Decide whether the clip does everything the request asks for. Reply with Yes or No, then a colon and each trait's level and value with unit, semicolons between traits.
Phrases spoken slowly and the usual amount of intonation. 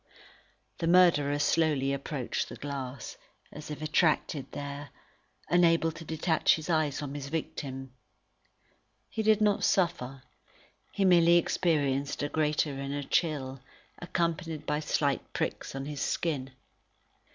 Yes: slow, 125 wpm; average, 3.1 semitones